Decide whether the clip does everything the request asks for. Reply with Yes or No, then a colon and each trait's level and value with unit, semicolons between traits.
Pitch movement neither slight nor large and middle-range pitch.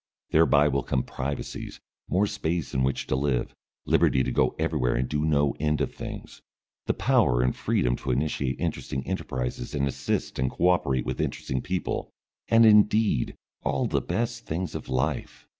No: average, 4.9 semitones; very low, 70 Hz